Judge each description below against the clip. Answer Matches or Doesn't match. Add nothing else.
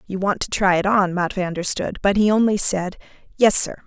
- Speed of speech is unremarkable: Doesn't match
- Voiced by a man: Doesn't match